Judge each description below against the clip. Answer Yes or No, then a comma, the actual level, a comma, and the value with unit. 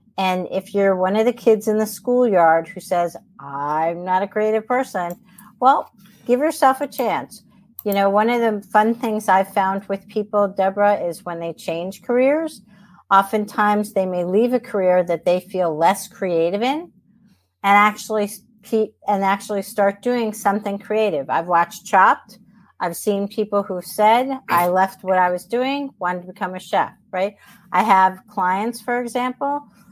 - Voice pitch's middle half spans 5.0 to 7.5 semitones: No, average, 2.9 semitones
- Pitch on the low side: No, high, 205 Hz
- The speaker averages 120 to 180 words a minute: Yes, average, 170 wpm